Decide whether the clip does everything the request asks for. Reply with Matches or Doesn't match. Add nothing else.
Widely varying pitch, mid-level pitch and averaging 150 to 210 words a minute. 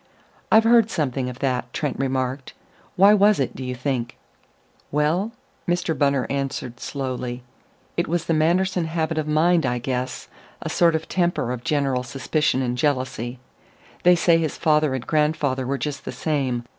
Doesn't match